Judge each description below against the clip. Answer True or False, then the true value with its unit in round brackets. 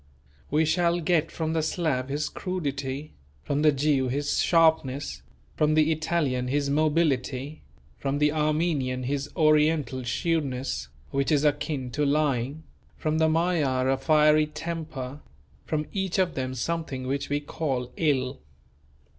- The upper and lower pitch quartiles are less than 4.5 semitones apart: True (2.9 semitones)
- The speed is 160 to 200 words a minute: False (140 wpm)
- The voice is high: False (150 Hz)